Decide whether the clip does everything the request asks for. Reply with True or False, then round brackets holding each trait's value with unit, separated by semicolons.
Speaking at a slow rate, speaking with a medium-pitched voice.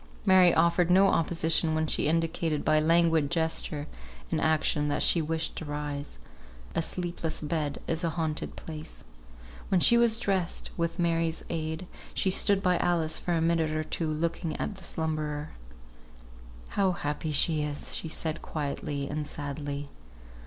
False (155 wpm; 160 Hz)